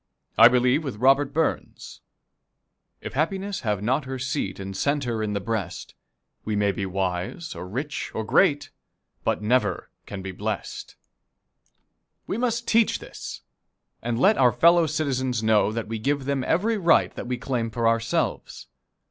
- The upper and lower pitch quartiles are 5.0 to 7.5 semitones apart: Yes, wide, 5.5 semitones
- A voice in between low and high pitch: No, low, 125 Hz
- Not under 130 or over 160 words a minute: Yes, average, 155 wpm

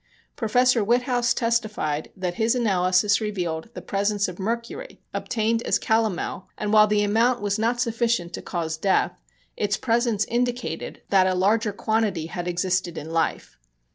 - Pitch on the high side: Yes, high, 210 Hz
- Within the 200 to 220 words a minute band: No, average, 150 wpm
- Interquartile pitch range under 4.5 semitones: Yes, average, 4.0 semitones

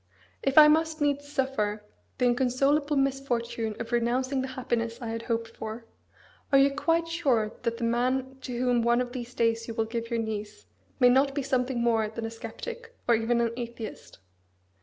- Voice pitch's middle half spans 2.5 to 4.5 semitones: Yes, average, 2.9 semitones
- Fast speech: No, average, 185 wpm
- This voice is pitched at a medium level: No, high, 245 Hz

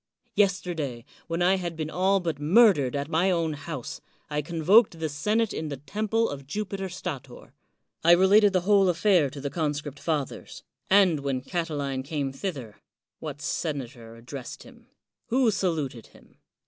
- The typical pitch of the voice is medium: Yes, medium, 160 Hz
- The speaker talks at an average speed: Yes, average, 160 wpm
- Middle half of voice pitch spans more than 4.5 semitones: Yes, average, 5.2 semitones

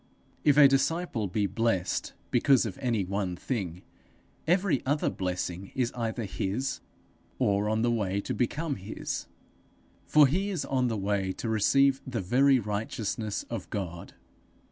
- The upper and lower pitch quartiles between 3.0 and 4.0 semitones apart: No, wide, 5.5 semitones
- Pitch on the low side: Yes, low, 115 Hz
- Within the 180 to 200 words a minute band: No, average, 145 wpm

